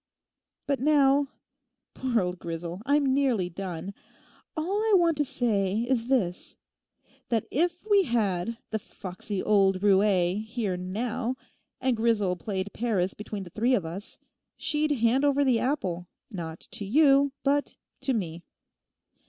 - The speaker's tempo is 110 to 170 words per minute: Yes, average, 140 wpm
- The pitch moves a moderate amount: No, wide, 6.4 semitones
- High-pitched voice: Yes, high, 225 Hz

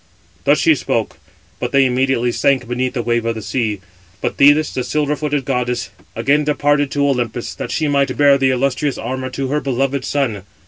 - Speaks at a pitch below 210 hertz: Yes, low, 135 Hz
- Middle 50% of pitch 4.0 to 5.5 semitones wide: No, narrow, 2.6 semitones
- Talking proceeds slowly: No, average, 190 wpm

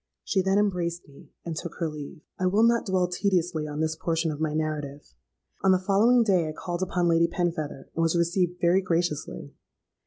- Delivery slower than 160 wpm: No, average, 195 wpm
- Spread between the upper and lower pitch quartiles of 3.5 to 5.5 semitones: No, average, 2.8 semitones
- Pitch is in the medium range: Yes, medium, 170 Hz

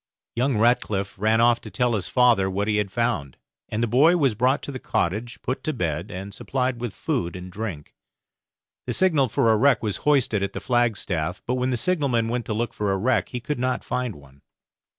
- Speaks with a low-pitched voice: Yes, low, 115 Hz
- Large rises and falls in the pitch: No, average, 4.2 semitones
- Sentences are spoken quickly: Yes, fast, 215 wpm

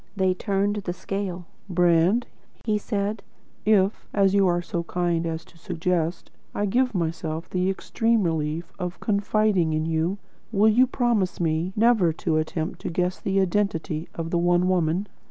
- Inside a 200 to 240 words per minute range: No, average, 165 wpm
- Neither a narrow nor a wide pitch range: Yes, average, 3.3 semitones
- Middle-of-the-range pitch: Yes, medium, 180 Hz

